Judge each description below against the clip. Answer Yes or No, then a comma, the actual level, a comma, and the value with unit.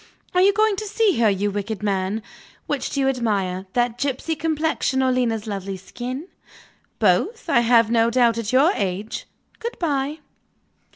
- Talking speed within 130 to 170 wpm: Yes, average, 165 wpm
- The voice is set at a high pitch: Yes, high, 245 Hz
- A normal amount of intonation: No, wide, 6.3 semitones